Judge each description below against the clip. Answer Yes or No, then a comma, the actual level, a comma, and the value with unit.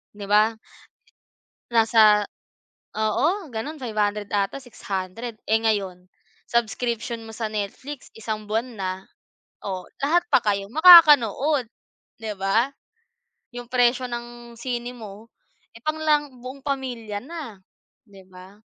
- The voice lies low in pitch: No, high, 230 Hz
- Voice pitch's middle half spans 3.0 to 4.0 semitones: Yes, average, 3.5 semitones